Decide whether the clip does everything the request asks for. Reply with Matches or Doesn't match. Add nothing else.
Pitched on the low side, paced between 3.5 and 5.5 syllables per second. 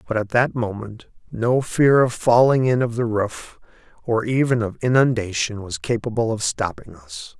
Matches